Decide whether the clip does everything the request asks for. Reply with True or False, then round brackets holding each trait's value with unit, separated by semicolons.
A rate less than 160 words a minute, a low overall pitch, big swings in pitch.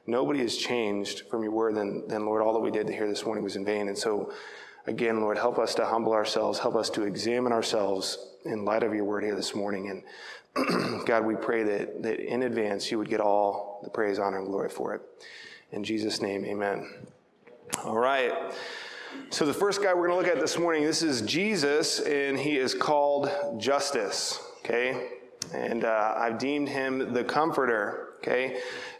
False (195 wpm; 115 Hz; 7.3 semitones)